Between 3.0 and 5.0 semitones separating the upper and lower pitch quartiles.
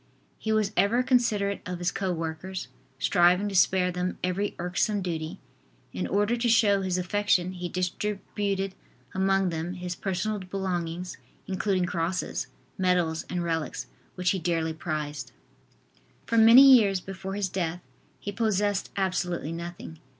No: narrow, 2.4 semitones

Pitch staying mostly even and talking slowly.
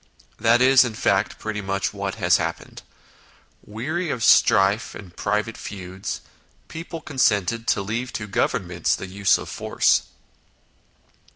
No: average, 3.3 semitones; slow, 130 wpm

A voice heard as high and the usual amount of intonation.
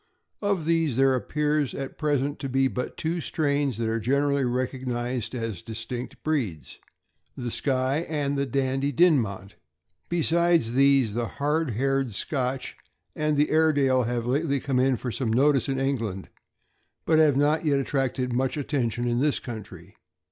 No: low, 135 Hz; average, 3.1 semitones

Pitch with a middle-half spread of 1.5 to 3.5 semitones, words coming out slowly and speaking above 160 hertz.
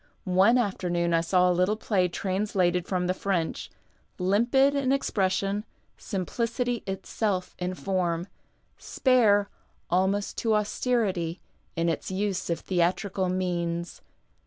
Yes: average, 2.8 semitones; slow, 120 wpm; high, 190 Hz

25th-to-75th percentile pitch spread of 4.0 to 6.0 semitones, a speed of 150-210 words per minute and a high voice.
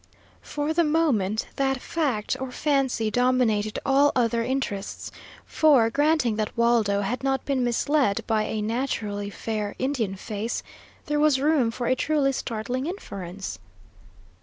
No: average, 4.4 semitones; slow, 135 wpm; high, 245 Hz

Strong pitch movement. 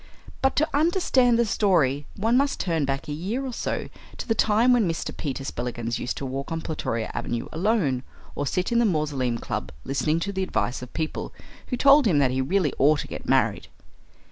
Yes: wide, 8.9 semitones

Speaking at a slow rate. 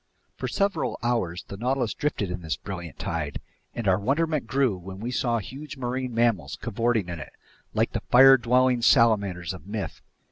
No: average, 175 wpm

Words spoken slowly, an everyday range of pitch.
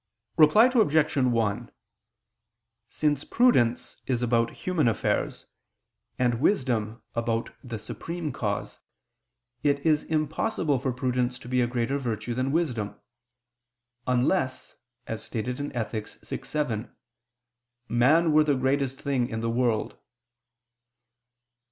Yes: slow, 115 wpm; average, 4.2 semitones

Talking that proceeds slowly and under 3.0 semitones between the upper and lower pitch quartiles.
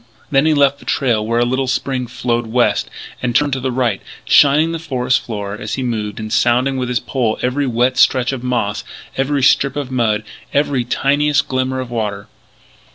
No: average, 195 wpm; narrow, 2.5 semitones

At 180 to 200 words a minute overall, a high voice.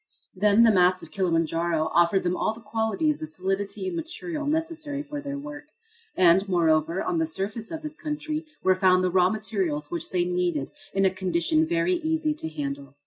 Yes: average, 190 wpm; high, 195 Hz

